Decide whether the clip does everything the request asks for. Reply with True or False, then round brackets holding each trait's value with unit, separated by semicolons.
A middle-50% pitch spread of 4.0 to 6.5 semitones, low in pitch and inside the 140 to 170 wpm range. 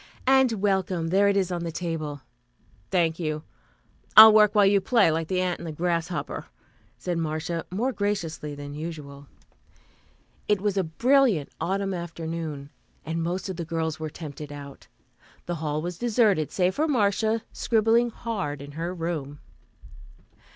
False (4.3 semitones; 175 Hz; 155 wpm)